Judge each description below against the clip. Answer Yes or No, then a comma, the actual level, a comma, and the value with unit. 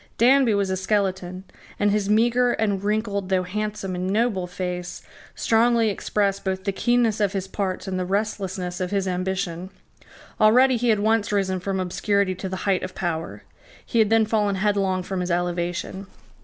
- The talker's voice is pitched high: Yes, high, 195 Hz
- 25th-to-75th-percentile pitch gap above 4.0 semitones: No, narrow, 2.5 semitones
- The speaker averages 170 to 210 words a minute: Yes, average, 175 wpm